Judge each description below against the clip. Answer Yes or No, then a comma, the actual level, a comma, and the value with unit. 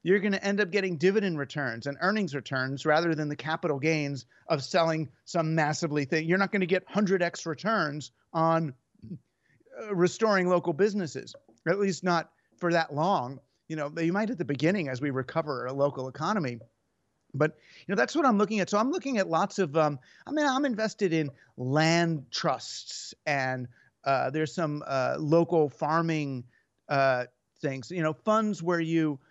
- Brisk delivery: No, average, 180 wpm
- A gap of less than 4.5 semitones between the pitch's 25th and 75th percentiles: No, average, 5.0 semitones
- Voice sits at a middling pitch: Yes, medium, 160 Hz